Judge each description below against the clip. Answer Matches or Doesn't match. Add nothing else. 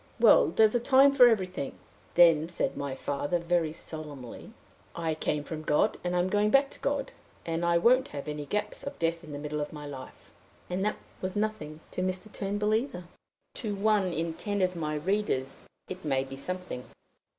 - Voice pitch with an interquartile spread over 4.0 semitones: Matches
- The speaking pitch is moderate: Matches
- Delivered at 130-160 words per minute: Doesn't match